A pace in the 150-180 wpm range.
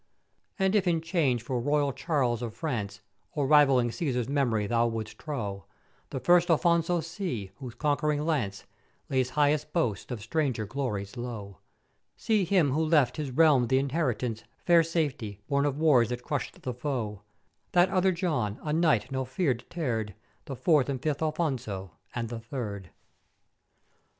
Yes: average, 155 wpm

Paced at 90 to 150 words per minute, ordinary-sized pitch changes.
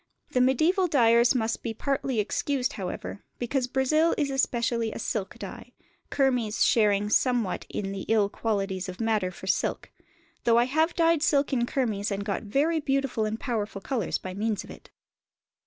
No: average, 170 wpm; average, 4.5 semitones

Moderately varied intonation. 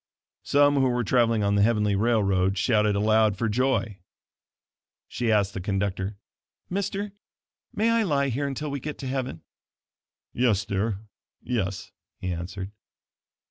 Yes: average, 5.0 semitones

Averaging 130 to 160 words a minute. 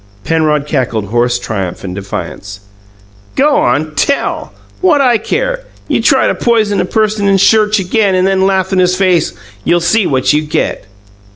No: average, 170 wpm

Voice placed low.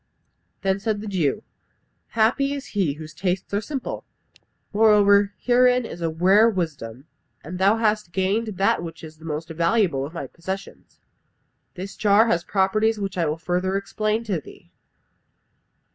No: high, 195 Hz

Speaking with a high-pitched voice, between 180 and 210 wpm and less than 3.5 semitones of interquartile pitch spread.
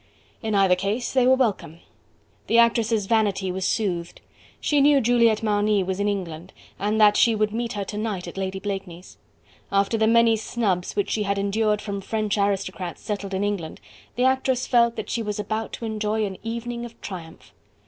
Yes: high, 210 Hz; average, 190 wpm; average, 2.7 semitones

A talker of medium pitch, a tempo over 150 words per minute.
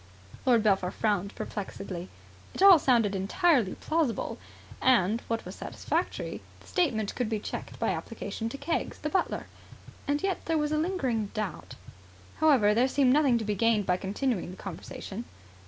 No: high, 230 Hz; average, 160 wpm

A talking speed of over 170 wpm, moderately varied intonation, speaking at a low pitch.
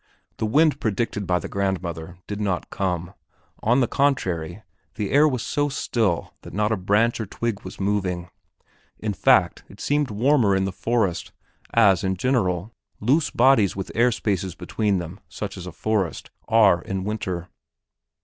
No: average, 160 wpm; average, 4.1 semitones; low, 105 Hz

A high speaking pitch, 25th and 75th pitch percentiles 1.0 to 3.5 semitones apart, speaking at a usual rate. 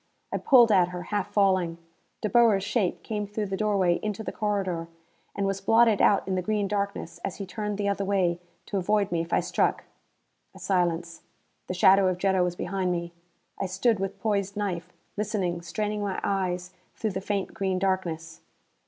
Yes: high, 195 Hz; narrow, 2.4 semitones; average, 190 wpm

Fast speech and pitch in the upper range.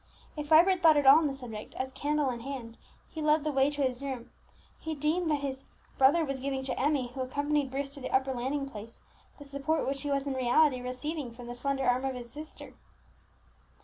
Yes: fast, 220 wpm; very high, 275 Hz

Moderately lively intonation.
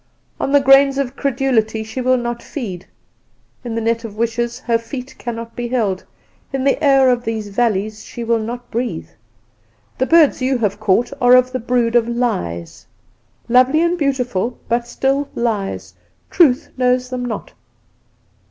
No: narrow, 2.3 semitones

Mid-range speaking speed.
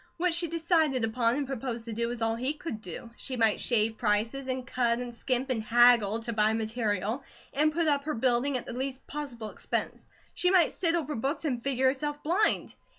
No: fast, 210 wpm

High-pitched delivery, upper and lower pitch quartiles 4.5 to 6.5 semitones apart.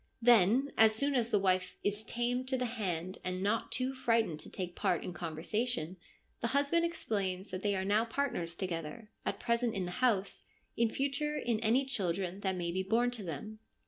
Yes: high, 215 Hz; average, 4.9 semitones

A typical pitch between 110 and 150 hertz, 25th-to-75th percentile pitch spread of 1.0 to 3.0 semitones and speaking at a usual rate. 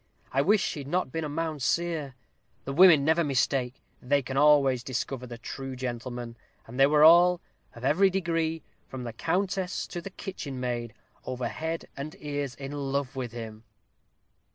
No: medium, 140 Hz; average, 4.3 semitones; average, 165 wpm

